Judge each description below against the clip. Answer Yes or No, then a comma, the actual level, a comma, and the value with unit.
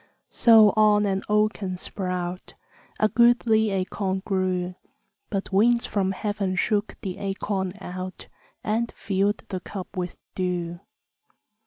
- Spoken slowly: Yes, slow, 120 wpm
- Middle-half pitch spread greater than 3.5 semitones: No, narrow, 2.4 semitones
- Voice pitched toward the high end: Yes, high, 195 Hz